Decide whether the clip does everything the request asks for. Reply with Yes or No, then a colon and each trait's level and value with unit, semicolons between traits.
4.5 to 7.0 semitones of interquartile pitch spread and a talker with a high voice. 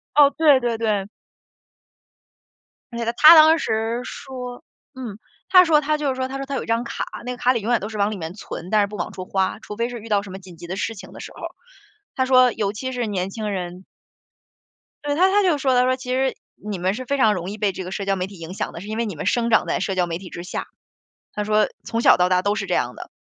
Yes: average, 4.9 semitones; high, 220 Hz